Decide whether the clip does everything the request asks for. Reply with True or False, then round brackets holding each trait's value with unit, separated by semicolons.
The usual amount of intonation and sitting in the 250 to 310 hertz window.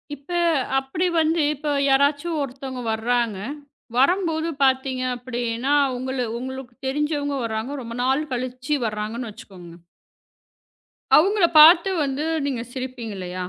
True (3.3 semitones; 265 Hz)